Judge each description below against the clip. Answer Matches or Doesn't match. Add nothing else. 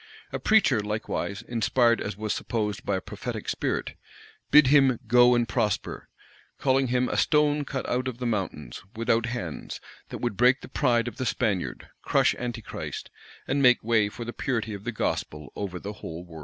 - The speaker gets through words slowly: Doesn't match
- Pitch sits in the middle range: Doesn't match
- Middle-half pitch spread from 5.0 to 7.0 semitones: Doesn't match